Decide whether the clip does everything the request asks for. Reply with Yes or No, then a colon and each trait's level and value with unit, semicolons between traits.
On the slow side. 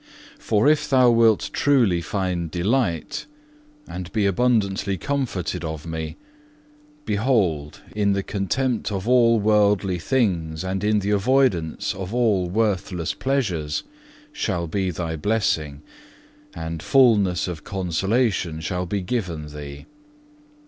Yes: slow, 120 wpm